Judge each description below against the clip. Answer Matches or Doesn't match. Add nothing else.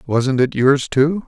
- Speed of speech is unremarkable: Matches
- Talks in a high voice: Doesn't match